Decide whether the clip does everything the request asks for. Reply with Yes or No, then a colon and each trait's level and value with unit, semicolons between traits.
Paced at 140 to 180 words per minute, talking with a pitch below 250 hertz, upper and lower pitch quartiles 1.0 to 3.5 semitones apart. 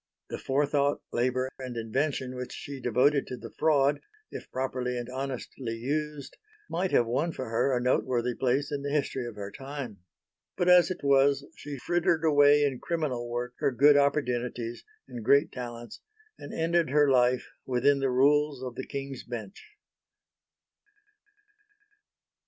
Yes: average, 150 wpm; low, 135 Hz; average, 2.8 semitones